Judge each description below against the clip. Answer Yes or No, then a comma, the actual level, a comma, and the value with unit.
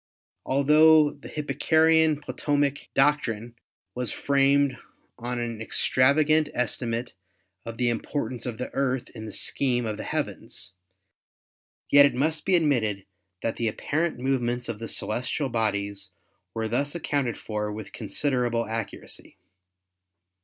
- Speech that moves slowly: Yes, slow, 130 wpm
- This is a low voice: Yes, low, 125 Hz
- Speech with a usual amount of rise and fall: Yes, average, 4.1 semitones